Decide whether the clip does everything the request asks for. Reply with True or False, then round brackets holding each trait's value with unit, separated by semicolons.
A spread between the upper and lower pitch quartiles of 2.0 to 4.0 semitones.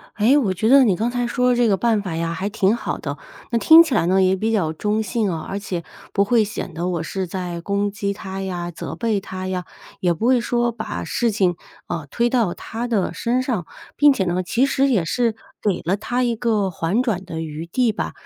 False (4.6 semitones)